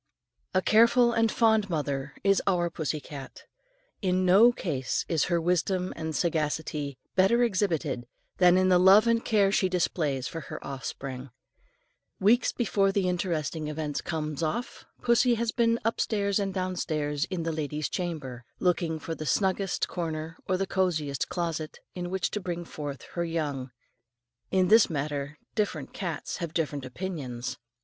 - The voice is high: No, medium, 175 Hz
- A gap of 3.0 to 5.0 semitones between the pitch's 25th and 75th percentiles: Yes, average, 4.3 semitones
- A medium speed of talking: Yes, average, 155 wpm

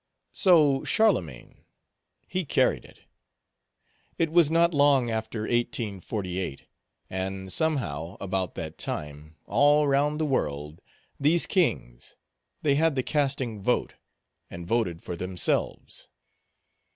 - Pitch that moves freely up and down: Yes, wide, 8.5 semitones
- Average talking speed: No, slow, 110 wpm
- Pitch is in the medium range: No, low, 120 Hz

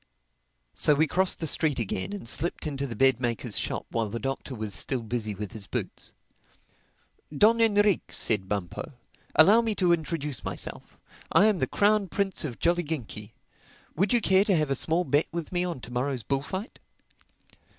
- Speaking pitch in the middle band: Yes, medium, 150 Hz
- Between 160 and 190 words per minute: Yes, average, 175 wpm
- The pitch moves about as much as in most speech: No, wide, 7.8 semitones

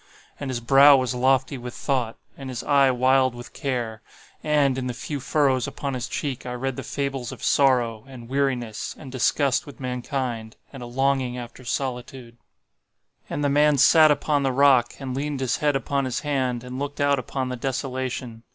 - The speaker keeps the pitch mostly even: Yes, narrow, 2.1 semitones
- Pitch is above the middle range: No, low, 130 Hz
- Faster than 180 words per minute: Yes, average, 190 wpm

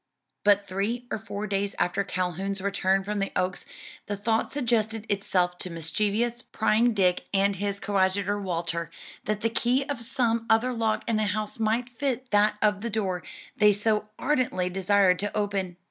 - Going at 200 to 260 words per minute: No, average, 170 wpm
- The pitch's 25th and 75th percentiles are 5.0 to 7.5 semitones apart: No, narrow, 2.6 semitones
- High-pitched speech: Yes, high, 205 Hz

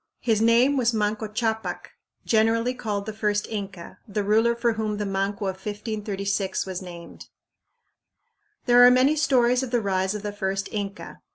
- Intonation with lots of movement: No, average, 2.7 semitones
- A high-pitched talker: Yes, high, 215 Hz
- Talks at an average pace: Yes, average, 165 wpm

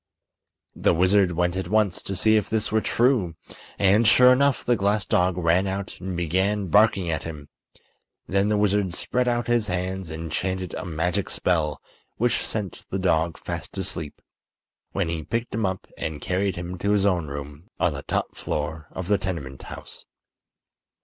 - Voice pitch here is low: Yes, very low, 95 Hz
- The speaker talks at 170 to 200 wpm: Yes, average, 175 wpm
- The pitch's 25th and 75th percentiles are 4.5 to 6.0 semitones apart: No, average, 3.6 semitones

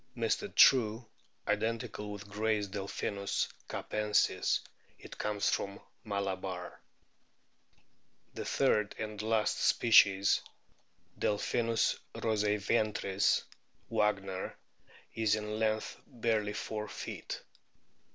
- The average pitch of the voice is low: Yes, low, 105 Hz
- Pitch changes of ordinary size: No, narrow, 1.6 semitones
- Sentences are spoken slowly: Yes, slow, 95 wpm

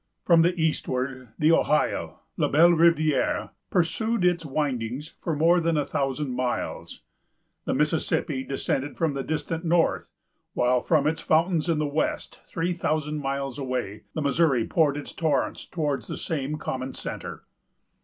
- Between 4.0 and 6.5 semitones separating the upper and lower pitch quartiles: No, average, 3.4 semitones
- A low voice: No, medium, 150 Hz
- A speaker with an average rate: Yes, average, 145 wpm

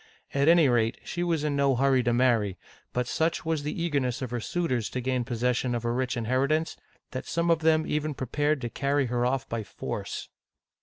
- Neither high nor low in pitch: No, low, 130 Hz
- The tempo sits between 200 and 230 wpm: Yes, fast, 205 wpm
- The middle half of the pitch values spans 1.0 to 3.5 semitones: No, average, 3.9 semitones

